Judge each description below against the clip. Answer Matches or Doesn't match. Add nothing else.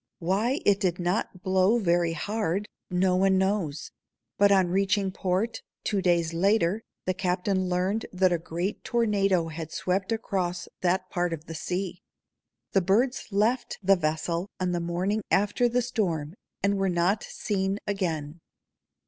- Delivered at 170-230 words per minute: Doesn't match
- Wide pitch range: Doesn't match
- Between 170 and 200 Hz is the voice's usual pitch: Matches